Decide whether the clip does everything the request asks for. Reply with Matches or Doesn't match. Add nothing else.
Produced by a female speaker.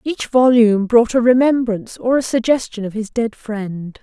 Matches